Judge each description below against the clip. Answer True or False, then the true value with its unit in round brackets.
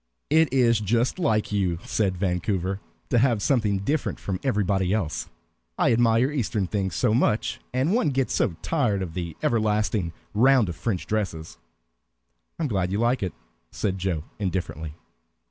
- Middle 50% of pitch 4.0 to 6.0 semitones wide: True (4.6 semitones)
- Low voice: True (105 Hz)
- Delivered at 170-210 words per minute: False (160 wpm)